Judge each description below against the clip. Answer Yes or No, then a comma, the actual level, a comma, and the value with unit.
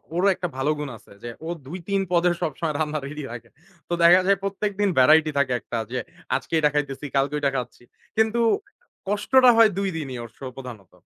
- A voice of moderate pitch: Yes, medium, 155 Hz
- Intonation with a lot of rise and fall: Yes, wide, 6.2 semitones